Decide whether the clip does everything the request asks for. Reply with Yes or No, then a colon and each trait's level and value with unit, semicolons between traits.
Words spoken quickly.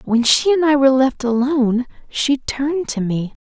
No: average, 195 wpm